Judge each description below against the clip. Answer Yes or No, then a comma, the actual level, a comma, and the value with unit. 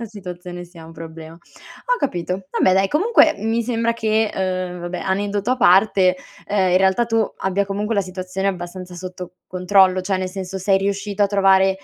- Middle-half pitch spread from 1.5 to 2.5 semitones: Yes, narrow, 2.0 semitones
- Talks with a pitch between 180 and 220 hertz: Yes, high, 190 Hz